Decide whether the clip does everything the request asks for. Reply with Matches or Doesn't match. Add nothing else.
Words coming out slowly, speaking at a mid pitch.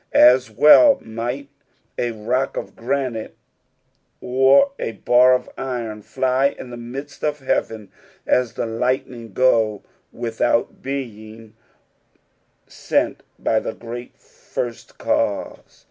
Doesn't match